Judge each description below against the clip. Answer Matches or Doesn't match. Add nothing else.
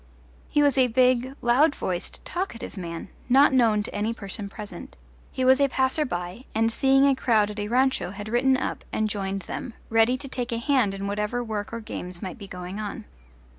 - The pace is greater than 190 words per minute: Matches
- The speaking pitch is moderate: Doesn't match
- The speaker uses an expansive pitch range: Doesn't match